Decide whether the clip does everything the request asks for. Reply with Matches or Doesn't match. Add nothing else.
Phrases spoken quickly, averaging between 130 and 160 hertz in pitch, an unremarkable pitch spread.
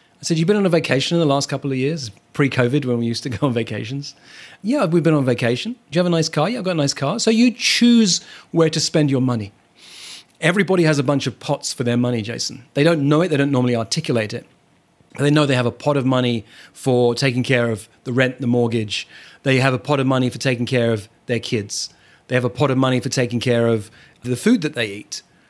Matches